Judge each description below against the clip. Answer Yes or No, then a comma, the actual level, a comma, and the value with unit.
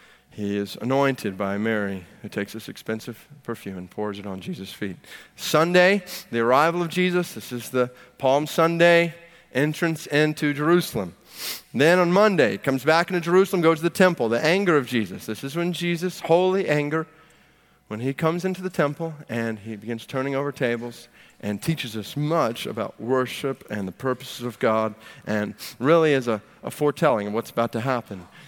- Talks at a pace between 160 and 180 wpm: Yes, average, 175 wpm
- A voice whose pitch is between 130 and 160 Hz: Yes, low, 135 Hz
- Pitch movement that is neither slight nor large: No, wide, 6.7 semitones